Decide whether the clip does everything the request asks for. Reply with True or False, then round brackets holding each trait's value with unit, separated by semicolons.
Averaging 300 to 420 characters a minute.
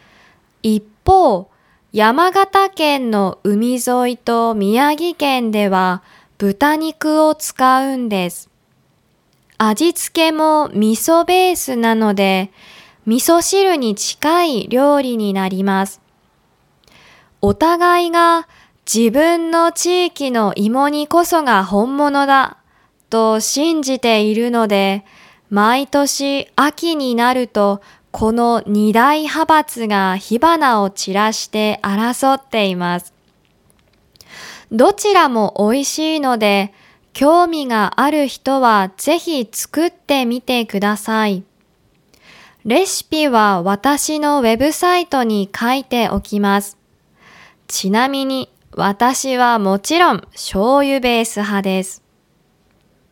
False (190 characters per minute)